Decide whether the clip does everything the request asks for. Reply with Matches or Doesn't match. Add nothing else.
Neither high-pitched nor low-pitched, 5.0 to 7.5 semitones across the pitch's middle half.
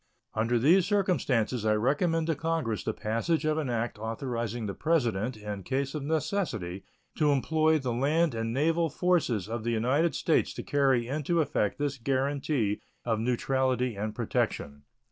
Doesn't match